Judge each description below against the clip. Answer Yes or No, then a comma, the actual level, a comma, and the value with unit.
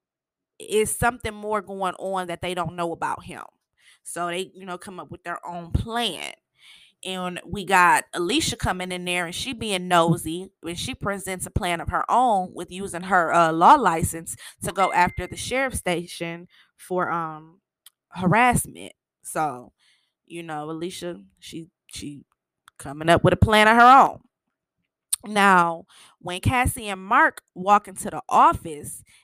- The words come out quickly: No, average, 160 wpm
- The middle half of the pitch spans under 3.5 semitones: Yes, average, 2.8 semitones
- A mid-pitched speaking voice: Yes, medium, 180 Hz